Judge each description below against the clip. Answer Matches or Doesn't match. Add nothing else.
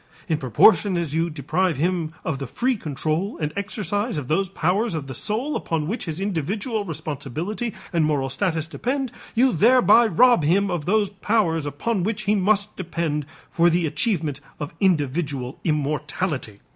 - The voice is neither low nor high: Matches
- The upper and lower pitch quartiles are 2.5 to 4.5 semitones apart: Doesn't match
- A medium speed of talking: Matches